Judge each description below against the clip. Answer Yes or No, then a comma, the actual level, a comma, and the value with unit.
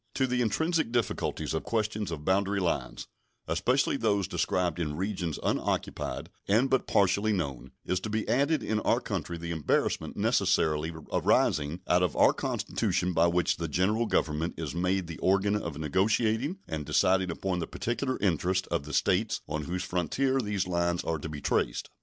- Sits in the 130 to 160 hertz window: No, very low, 90 Hz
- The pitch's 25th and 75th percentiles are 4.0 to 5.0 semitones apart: Yes, average, 4.5 semitones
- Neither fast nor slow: Yes, average, 170 wpm